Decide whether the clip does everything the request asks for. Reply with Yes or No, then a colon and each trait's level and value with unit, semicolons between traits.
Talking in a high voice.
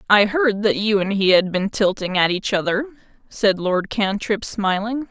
Yes: high, 210 Hz